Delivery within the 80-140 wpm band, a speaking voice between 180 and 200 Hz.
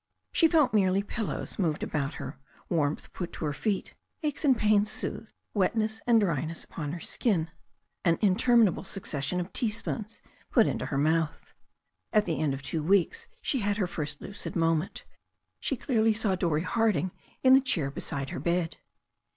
No: average, 165 wpm; medium, 185 Hz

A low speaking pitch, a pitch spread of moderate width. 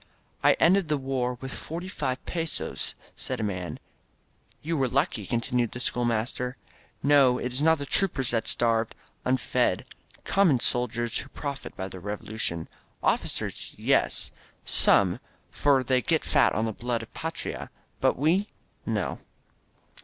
Yes: low, 130 Hz; average, 3.8 semitones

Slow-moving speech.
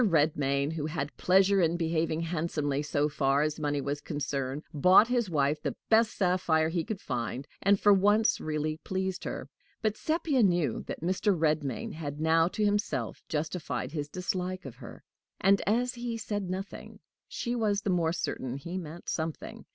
No: average, 170 wpm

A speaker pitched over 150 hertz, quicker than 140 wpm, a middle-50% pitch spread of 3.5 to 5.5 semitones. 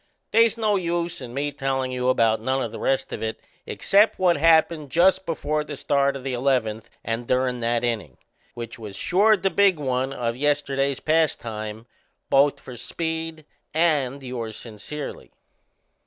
No: low, 135 Hz; average, 160 wpm; average, 5.0 semitones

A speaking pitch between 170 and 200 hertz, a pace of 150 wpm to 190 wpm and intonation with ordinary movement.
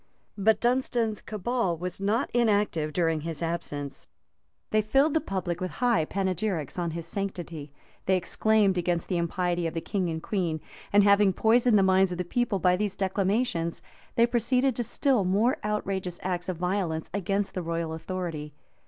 Yes: high, 190 Hz; average, 170 wpm; average, 3.8 semitones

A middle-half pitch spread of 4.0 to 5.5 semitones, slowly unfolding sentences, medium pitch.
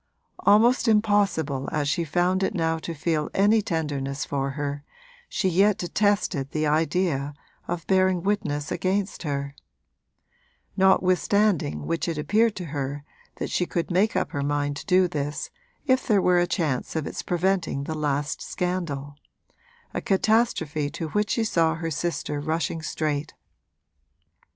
No: average, 4.6 semitones; average, 145 wpm; medium, 165 Hz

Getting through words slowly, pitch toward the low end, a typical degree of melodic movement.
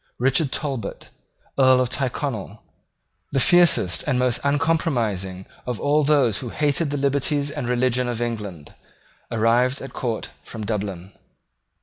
Yes: slow, 130 wpm; low, 125 Hz; average, 4.1 semitones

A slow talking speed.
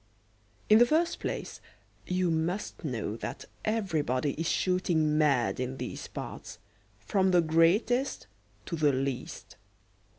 Yes: slow, 125 wpm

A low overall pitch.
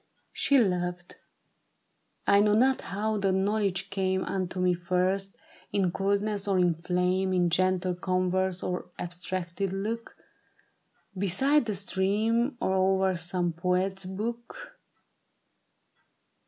No: high, 190 Hz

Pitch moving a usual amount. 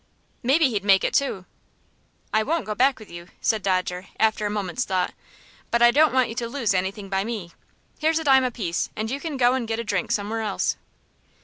Yes: average, 4.8 semitones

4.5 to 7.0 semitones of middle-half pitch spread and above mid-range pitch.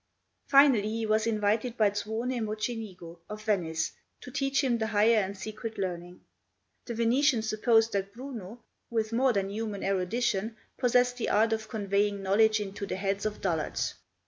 No: narrow, 2.6 semitones; high, 215 Hz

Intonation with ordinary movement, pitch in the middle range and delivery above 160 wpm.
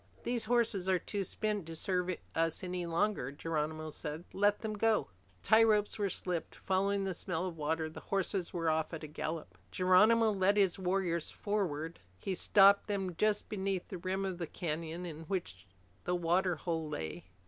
Yes: average, 3.6 semitones; medium, 180 Hz; average, 180 wpm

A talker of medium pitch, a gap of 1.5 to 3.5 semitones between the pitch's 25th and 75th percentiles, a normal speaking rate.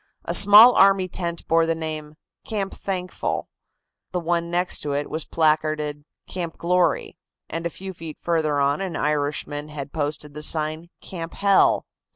Yes: medium, 165 Hz; average, 3.0 semitones; average, 160 wpm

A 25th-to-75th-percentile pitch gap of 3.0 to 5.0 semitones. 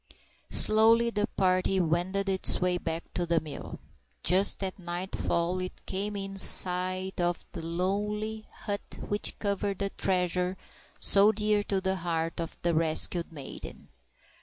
No: narrow, 2.5 semitones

